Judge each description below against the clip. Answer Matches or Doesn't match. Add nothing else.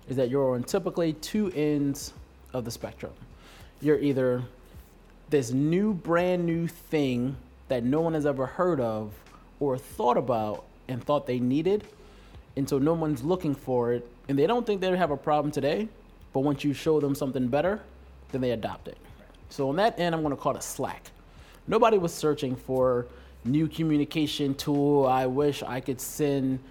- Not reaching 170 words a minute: Doesn't match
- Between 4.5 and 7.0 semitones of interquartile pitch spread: Doesn't match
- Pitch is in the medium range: Matches